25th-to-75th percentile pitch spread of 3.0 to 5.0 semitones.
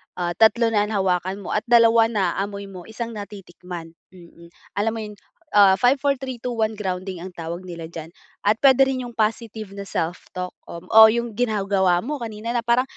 Yes: average, 4.0 semitones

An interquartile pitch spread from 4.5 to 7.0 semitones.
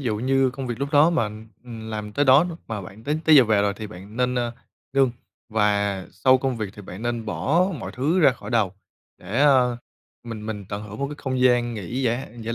No: average, 4.0 semitones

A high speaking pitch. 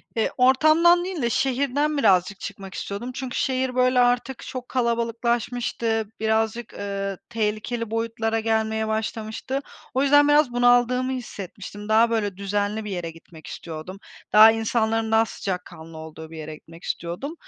Yes: high, 225 Hz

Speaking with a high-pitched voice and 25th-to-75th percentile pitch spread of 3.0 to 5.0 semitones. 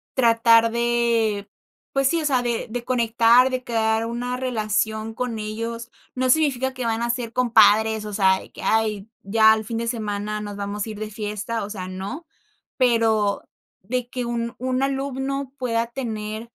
No: high, 230 Hz; narrow, 2.5 semitones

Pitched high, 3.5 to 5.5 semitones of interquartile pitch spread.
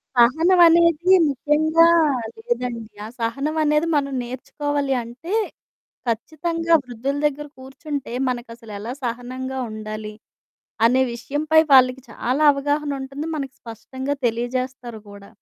Yes: very high, 265 Hz; average, 3.9 semitones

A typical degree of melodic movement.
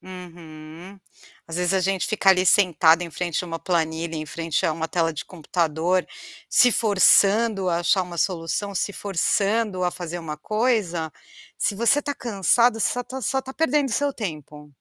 Yes: average, 4.3 semitones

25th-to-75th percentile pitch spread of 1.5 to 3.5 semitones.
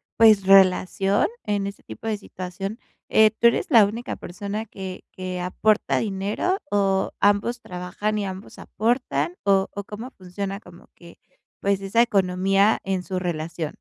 Yes: narrow, 2.4 semitones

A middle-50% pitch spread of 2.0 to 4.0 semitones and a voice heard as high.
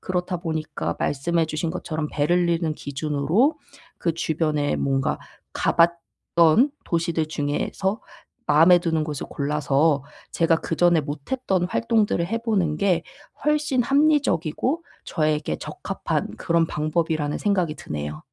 No: average, 3.4 semitones; medium, 165 Hz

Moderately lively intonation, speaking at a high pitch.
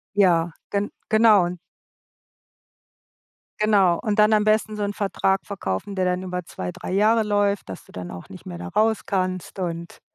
Yes: average, 3.4 semitones; high, 195 Hz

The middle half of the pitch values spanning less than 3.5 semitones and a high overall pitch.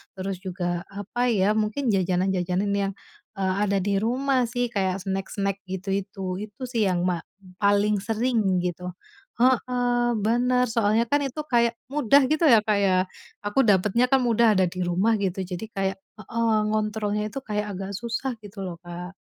No: average, 3.8 semitones; high, 205 Hz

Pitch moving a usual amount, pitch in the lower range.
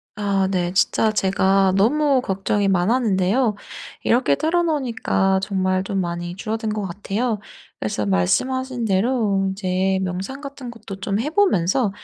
No: average, 4.4 semitones; high, 200 Hz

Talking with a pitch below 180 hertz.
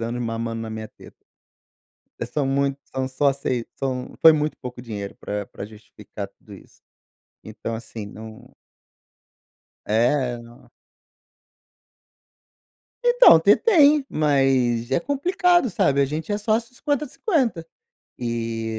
Yes: low, 135 Hz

